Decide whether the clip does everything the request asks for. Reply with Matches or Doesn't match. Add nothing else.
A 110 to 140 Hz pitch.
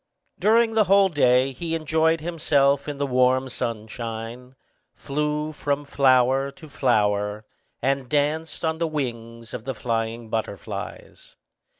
Matches